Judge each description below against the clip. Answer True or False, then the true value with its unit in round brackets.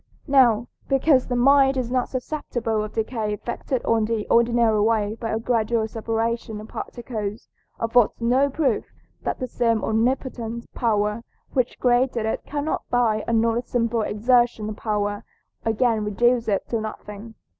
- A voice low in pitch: False (230 Hz)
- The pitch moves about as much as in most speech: False (2.2 semitones)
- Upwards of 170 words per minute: False (145 wpm)